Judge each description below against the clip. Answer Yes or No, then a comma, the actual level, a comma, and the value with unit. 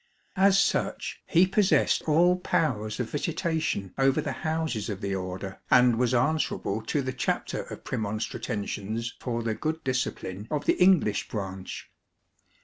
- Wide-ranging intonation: Yes, wide, 7.2 semitones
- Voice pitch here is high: No, low, 125 Hz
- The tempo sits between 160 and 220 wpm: No, average, 140 wpm